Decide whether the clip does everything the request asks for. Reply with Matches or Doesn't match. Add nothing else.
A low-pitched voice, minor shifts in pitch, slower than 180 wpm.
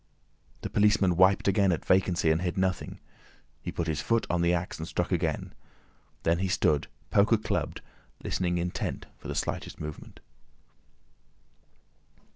Matches